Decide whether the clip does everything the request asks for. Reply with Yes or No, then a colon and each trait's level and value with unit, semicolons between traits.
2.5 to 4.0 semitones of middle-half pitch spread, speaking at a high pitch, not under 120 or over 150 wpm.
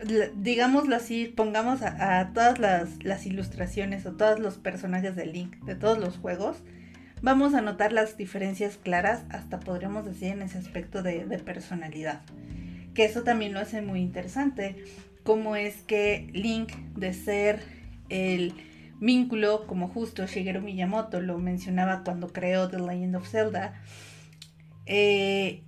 Yes: average, 3.0 semitones; high, 195 Hz; average, 145 wpm